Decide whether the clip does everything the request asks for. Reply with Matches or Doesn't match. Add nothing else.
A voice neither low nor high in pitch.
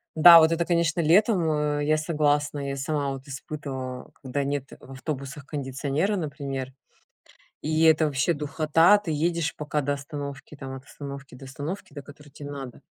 Matches